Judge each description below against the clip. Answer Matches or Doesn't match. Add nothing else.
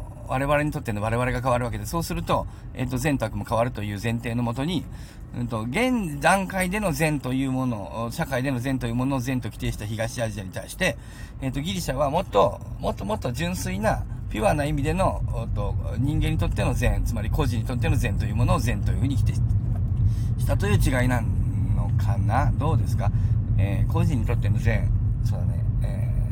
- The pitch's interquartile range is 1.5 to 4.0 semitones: Matches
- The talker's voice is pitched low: Matches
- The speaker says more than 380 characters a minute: Matches